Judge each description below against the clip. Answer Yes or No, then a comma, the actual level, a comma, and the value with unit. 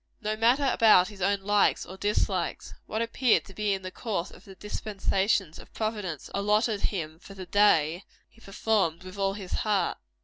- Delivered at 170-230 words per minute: Yes, average, 180 wpm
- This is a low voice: No, high, 200 Hz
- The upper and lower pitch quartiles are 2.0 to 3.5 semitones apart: Yes, narrow, 2.5 semitones